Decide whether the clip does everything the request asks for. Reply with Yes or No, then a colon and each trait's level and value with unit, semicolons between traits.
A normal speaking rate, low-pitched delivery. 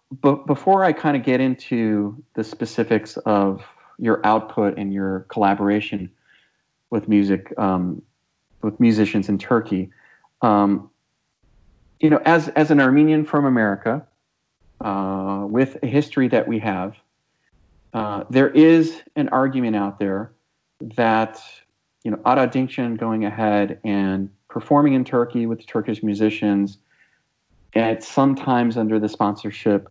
No: slow, 130 wpm; low, 110 Hz